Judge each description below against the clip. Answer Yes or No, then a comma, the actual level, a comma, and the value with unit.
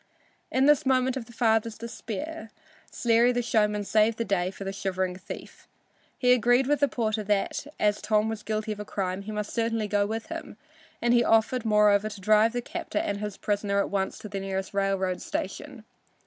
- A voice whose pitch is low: No, high, 215 Hz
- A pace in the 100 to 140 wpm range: No, average, 200 wpm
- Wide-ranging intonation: No, narrow, 2.6 semitones